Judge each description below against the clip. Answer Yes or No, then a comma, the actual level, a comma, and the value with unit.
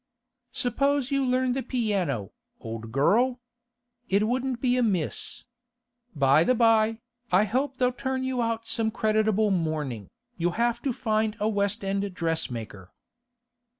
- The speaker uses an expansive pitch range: Yes, wide, 6.1 semitones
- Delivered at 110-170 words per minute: Yes, slow, 135 wpm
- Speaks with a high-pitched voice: Yes, high, 220 Hz